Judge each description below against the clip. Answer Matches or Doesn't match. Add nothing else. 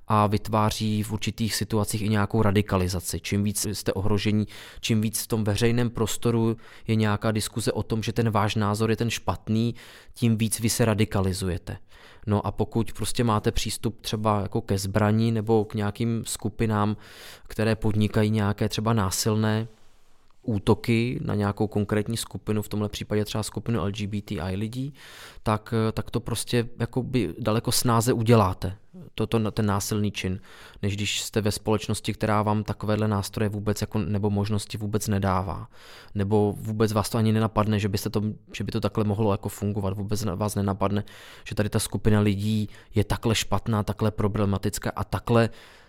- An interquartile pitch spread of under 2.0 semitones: Matches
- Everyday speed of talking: Matches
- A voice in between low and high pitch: Doesn't match